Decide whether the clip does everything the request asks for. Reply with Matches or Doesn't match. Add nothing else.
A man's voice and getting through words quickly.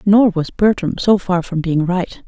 Doesn't match